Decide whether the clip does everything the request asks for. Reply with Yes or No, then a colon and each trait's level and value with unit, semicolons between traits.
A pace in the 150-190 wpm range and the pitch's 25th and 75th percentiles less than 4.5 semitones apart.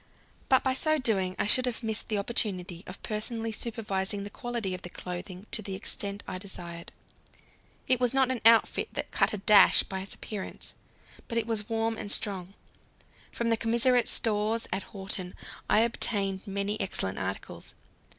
Yes: average, 170 wpm; average, 3.1 semitones